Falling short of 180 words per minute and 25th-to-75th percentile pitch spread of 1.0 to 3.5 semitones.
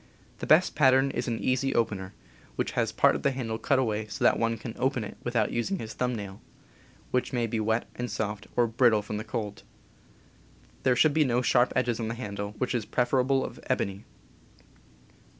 No: average, 200 wpm; average, 2.9 semitones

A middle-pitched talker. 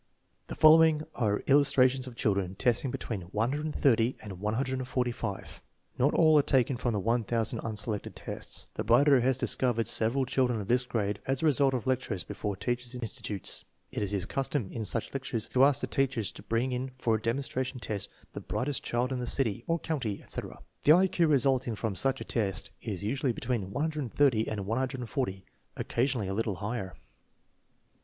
No: low, 125 Hz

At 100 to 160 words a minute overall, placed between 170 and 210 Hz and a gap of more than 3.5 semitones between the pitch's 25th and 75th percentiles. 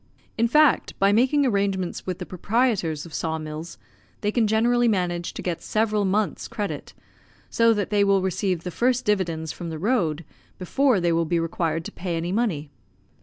No: average, 180 wpm; high, 190 Hz; average, 4.8 semitones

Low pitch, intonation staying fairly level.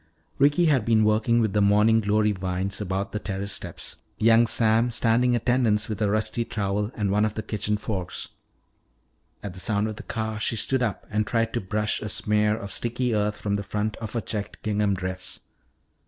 Yes: low, 105 Hz; narrow, 1.9 semitones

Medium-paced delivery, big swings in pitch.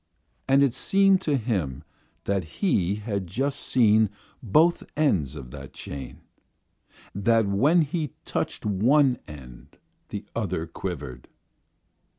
No: slow, 120 wpm; wide, 8.6 semitones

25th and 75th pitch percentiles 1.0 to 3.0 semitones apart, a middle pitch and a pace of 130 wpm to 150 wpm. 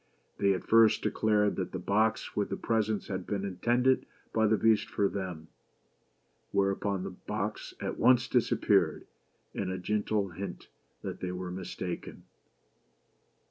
No: narrow, 2.6 semitones; low, 100 Hz; average, 140 wpm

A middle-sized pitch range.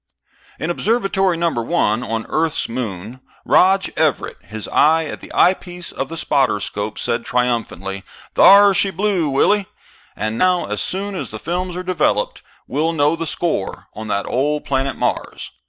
No: wide, 7.6 semitones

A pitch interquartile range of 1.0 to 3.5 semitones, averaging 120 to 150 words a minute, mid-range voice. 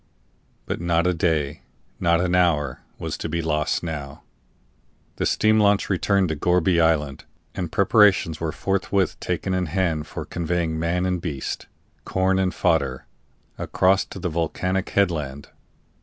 No: average, 2.8 semitones; average, 145 wpm; very low, 85 Hz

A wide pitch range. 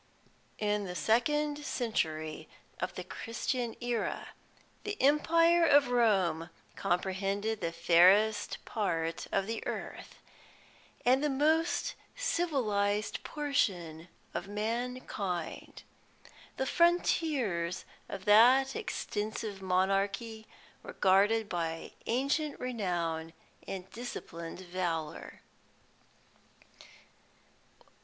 Yes: wide, 6.2 semitones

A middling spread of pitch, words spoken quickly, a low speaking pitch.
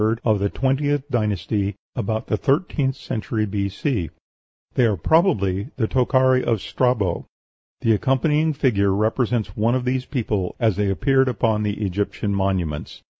No: average, 4.6 semitones; average, 140 wpm; low, 110 Hz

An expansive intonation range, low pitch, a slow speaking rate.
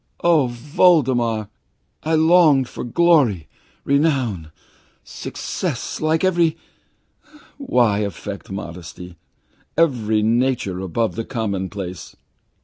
Yes: wide, 7.6 semitones; low, 120 Hz; slow, 85 wpm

